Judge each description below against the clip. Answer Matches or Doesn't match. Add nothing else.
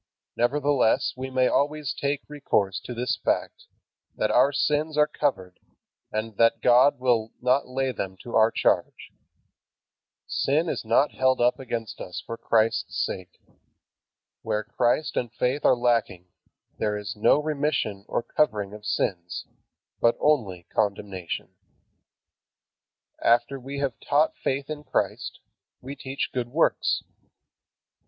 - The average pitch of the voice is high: Doesn't match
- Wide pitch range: Doesn't match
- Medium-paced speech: Doesn't match